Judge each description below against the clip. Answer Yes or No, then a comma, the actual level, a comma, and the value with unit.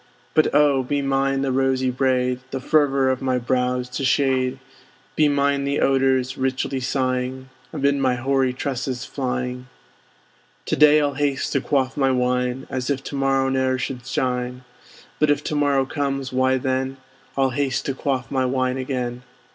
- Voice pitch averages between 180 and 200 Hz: No, low, 130 Hz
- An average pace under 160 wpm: No, average, 165 wpm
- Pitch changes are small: Yes, narrow, 1.3 semitones